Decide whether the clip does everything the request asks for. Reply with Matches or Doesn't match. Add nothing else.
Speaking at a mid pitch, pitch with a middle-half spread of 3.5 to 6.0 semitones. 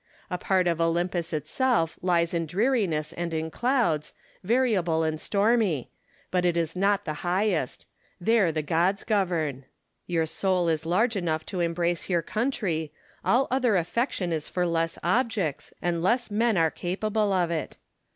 Matches